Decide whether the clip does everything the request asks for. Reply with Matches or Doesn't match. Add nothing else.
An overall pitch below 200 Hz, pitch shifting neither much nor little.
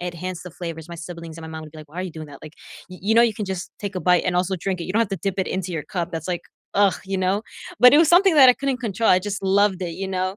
Matches